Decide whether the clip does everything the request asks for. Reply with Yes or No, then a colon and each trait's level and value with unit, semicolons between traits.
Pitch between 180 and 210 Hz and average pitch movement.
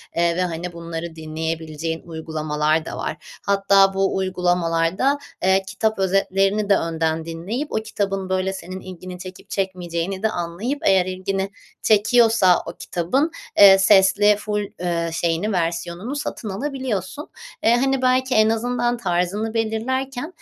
Yes: high, 190 Hz; average, 4.3 semitones